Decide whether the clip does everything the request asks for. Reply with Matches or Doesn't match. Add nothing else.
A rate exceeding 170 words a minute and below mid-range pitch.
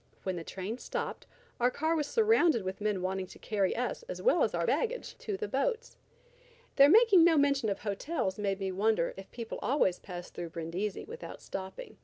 Doesn't match